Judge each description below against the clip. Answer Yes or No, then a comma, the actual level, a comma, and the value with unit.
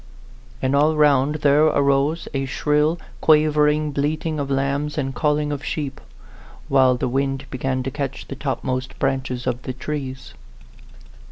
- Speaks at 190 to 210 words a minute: No, average, 145 wpm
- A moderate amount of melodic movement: No, narrow, 2.0 semitones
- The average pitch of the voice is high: No, medium, 140 Hz